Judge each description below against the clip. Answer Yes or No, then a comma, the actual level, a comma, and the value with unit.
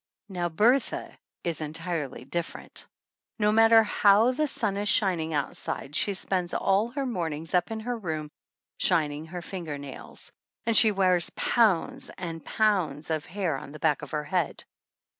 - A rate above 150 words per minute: Yes, average, 160 wpm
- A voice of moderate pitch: Yes, medium, 180 Hz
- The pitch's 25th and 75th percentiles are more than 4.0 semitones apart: Yes, average, 5.1 semitones